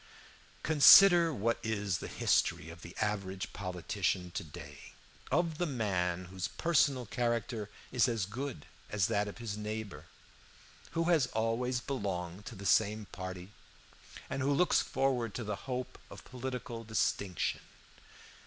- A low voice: Yes, low, 110 Hz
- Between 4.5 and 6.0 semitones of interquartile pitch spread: Yes, average, 5.1 semitones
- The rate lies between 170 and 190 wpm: No, average, 140 wpm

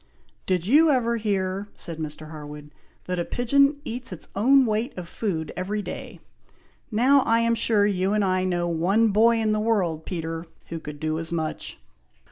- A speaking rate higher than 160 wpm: Yes, average, 180 wpm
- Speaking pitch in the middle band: No, high, 195 Hz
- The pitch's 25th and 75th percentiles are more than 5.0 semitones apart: Yes, wide, 5.5 semitones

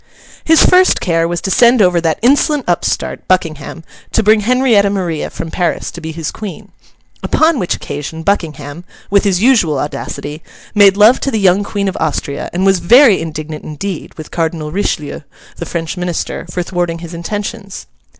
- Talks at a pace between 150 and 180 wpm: Yes, average, 165 wpm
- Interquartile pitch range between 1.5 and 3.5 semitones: No, average, 4.0 semitones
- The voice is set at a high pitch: No, medium, 180 Hz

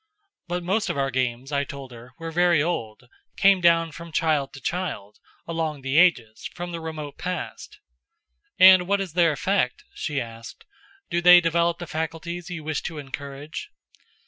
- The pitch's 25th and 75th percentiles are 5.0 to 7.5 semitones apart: No, average, 4.2 semitones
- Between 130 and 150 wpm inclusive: No, average, 170 wpm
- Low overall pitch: No, medium, 160 Hz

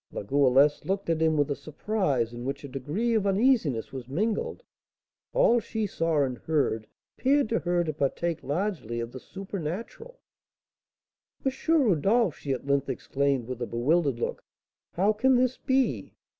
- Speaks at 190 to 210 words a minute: No, average, 160 wpm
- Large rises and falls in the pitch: Yes, wide, 7.8 semitones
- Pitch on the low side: No, medium, 160 Hz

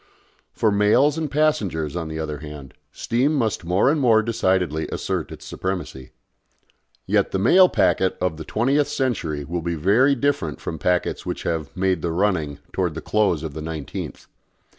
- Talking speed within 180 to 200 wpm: No, average, 170 wpm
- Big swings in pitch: Yes, wide, 6.8 semitones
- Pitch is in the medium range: No, very low, 95 Hz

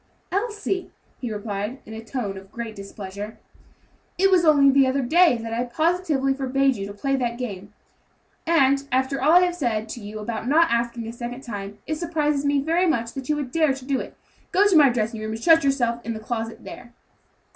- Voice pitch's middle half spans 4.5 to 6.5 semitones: Yes, average, 4.9 semitones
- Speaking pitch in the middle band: No, very high, 255 Hz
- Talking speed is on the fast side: Yes, fast, 215 wpm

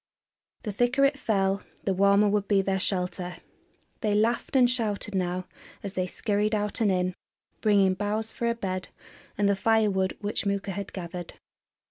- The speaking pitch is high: Yes, high, 200 Hz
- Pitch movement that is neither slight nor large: No, narrow, 2.2 semitones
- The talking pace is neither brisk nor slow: Yes, average, 170 wpm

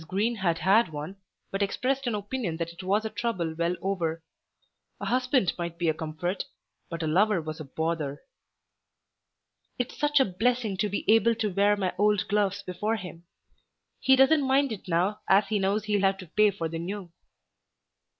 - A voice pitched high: Yes, high, 195 Hz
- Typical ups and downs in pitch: Yes, average, 4.3 semitones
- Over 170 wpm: Yes, average, 185 wpm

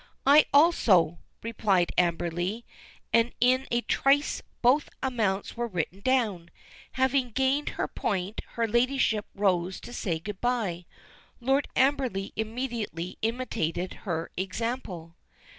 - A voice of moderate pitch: No, high, 225 Hz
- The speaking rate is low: Yes, slow, 115 wpm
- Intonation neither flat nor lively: No, wide, 5.8 semitones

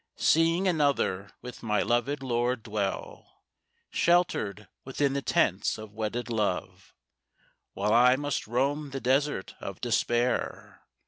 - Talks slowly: Yes, slow, 120 wpm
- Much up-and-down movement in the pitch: No, average, 4.7 semitones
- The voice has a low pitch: Yes, low, 120 Hz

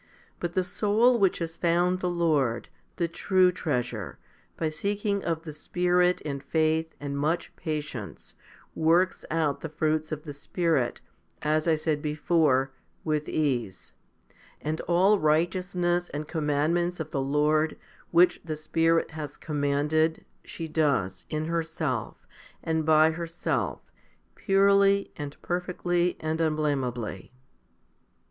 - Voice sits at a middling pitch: Yes, medium, 160 Hz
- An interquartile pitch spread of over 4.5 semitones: No, average, 2.7 semitones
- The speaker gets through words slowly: Yes, slow, 125 wpm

